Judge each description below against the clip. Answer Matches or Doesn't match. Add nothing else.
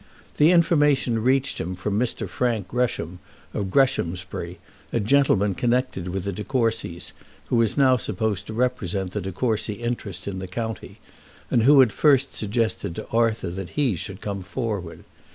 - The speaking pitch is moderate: Doesn't match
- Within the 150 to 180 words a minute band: Matches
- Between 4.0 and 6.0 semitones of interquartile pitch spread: Matches